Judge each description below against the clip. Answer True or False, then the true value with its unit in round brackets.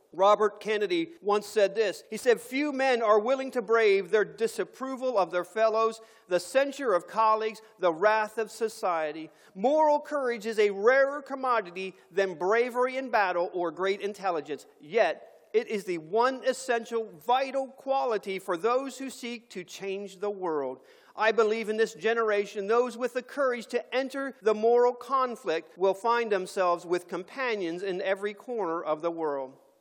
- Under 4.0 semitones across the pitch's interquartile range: False (4.3 semitones)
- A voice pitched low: False (220 Hz)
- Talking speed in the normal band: True (160 wpm)